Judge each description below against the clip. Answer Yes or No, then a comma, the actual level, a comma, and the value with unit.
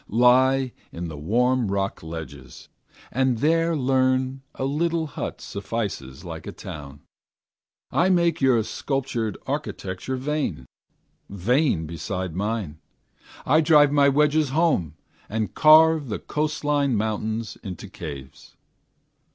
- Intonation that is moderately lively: No, wide, 7.7 semitones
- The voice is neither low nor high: No, low, 125 Hz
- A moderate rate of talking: No, slow, 115 wpm